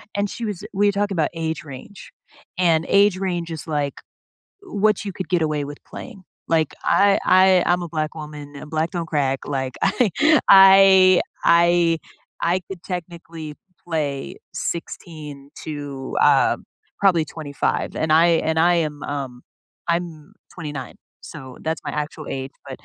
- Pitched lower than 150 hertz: No, medium, 165 Hz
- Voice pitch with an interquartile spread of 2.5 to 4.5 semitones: Yes, average, 3.8 semitones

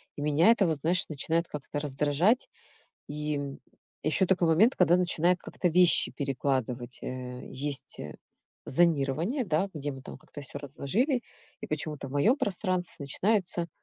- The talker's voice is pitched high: No, medium, 155 Hz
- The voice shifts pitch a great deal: No, average, 4.3 semitones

